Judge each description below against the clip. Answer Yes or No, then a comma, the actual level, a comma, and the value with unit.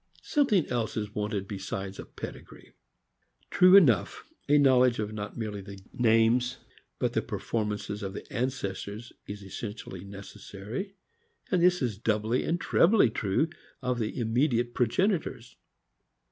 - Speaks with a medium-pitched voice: No, low, 115 Hz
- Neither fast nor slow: No, slow, 130 wpm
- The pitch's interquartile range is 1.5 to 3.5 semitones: No, average, 4.0 semitones